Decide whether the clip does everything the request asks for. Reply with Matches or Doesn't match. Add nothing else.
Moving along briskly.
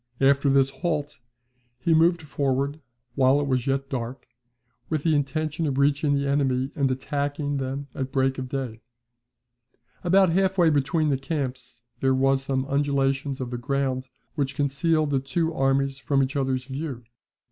Doesn't match